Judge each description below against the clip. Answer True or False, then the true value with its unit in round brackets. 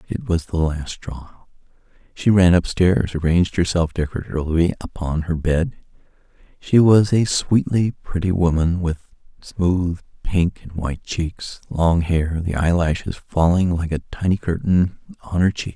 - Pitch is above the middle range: False (90 Hz)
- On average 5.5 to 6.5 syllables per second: False (4.4 syllables/s)